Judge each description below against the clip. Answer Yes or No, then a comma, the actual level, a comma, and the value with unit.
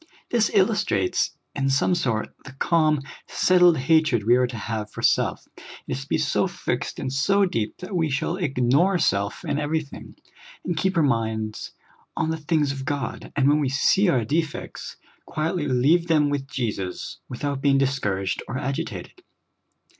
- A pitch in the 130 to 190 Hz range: Yes, medium, 140 Hz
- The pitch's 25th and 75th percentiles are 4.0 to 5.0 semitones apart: Yes, average, 4.5 semitones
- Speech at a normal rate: Yes, average, 170 wpm